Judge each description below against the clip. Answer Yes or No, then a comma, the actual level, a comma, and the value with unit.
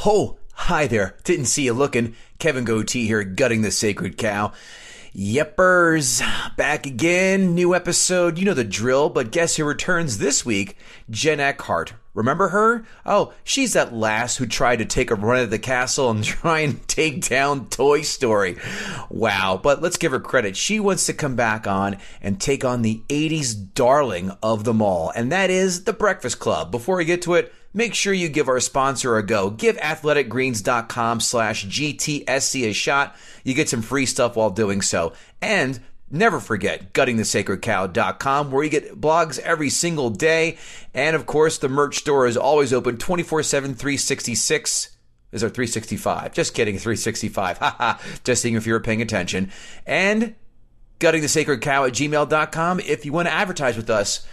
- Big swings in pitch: Yes, wide, 6.3 semitones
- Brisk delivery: No, average, 170 wpm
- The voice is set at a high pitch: No, medium, 140 Hz